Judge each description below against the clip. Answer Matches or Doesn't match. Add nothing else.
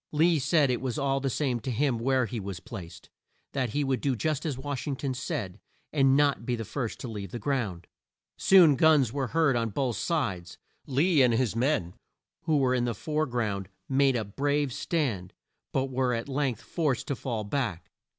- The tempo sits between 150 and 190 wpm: Doesn't match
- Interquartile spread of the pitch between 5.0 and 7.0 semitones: Doesn't match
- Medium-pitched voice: Doesn't match